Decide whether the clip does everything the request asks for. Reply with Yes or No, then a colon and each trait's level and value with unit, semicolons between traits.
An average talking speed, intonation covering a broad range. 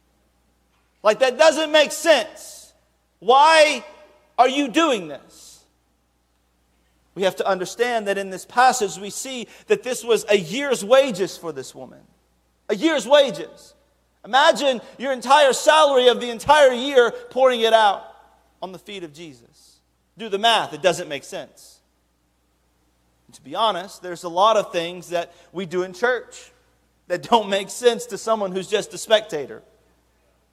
Yes: average, 155 wpm; wide, 7.9 semitones